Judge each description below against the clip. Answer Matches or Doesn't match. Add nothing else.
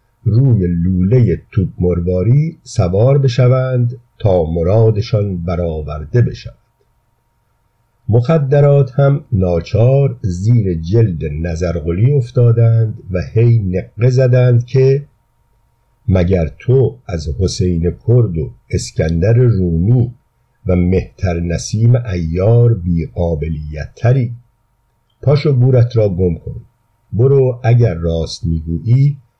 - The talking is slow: Matches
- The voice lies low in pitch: Matches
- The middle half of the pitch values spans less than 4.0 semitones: Doesn't match